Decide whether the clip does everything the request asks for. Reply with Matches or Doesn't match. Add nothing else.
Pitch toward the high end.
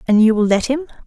Matches